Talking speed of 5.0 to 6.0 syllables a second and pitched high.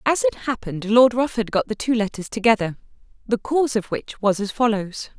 Yes: 5.6 syllables/s; high, 220 Hz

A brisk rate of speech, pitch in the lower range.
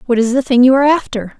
No: fast, 300 wpm; very high, 250 Hz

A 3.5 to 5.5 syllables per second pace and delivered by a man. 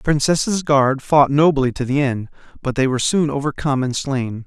Yes: 5.1 syllables/s; male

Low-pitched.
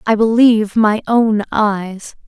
No: high, 215 Hz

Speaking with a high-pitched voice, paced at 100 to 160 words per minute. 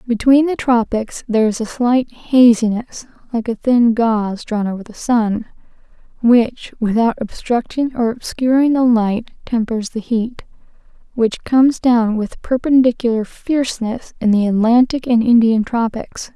Yes: high, 235 Hz; average, 140 wpm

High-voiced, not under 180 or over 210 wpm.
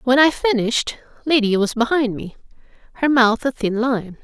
No: high, 245 Hz; average, 170 wpm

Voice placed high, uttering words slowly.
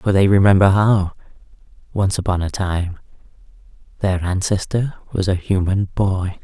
No: very low, 95 Hz; slow, 130 wpm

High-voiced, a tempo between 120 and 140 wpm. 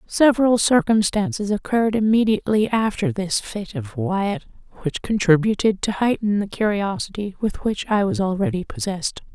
Yes: high, 205 Hz; slow, 135 wpm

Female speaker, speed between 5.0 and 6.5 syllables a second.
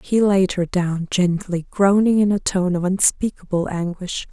No: female; 4.4 syllables/s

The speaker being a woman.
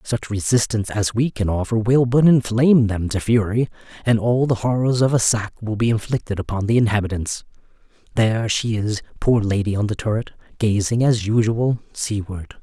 No: male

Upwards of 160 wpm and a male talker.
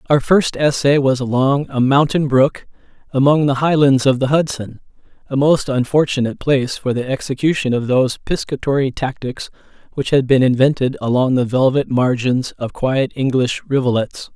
No: average, 150 wpm; male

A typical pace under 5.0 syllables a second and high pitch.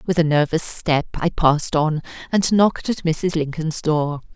No: 4.5 syllables/s; medium, 160 Hz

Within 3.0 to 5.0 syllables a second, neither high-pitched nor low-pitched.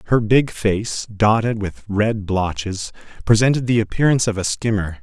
No: 4.8 syllables/s; low, 105 Hz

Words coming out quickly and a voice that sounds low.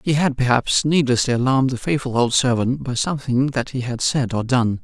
Yes: fast, 210 wpm; low, 130 Hz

